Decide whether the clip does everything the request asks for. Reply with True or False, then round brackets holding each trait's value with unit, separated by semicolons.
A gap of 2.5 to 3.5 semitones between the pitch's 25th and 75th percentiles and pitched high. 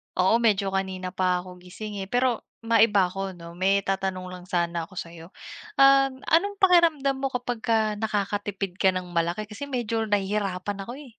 False (4.4 semitones; 200 Hz)